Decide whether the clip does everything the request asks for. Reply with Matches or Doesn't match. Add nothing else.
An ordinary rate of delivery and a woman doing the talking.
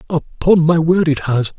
Doesn't match